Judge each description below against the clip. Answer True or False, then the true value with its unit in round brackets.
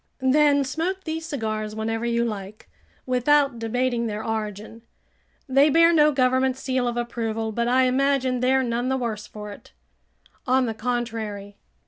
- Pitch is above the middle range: True (245 Hz)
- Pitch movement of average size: True (3.0 semitones)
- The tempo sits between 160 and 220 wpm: False (150 wpm)